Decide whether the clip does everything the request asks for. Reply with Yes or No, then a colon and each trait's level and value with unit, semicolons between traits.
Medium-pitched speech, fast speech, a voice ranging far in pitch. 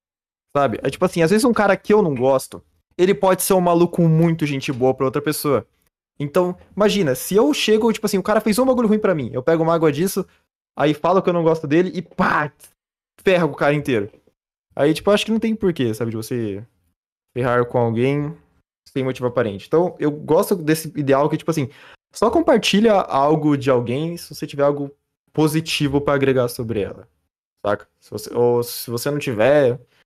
Yes: medium, 150 Hz; fast, 205 wpm; wide, 5.7 semitones